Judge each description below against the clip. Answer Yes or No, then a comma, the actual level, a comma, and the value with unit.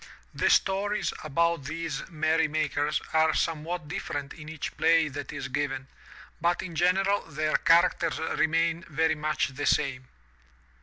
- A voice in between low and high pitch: Yes, medium, 160 Hz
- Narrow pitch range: Yes, narrow, 2.2 semitones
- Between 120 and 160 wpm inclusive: Yes, average, 140 wpm